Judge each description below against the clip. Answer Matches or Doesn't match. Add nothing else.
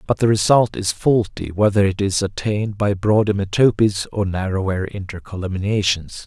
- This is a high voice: Doesn't match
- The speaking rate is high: Doesn't match